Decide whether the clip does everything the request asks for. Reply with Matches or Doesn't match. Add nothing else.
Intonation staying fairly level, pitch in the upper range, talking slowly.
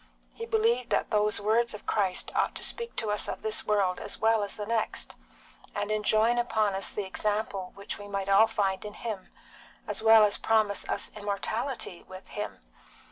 Doesn't match